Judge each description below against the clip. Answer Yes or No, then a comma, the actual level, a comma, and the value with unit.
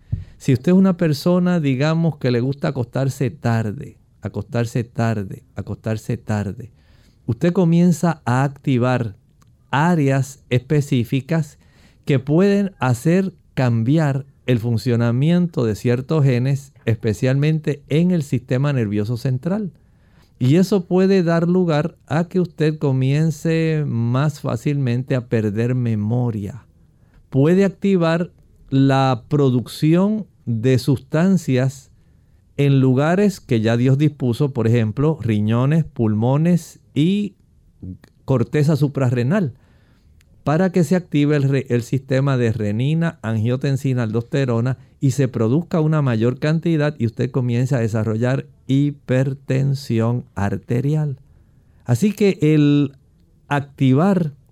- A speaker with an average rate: No, slow, 105 wpm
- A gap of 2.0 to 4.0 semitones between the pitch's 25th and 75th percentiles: No, average, 4.4 semitones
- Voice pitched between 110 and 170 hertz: Yes, low, 135 Hz